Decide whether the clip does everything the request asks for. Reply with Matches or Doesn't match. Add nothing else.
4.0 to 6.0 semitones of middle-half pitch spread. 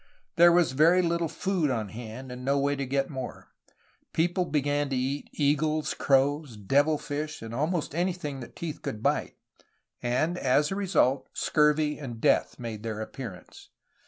Doesn't match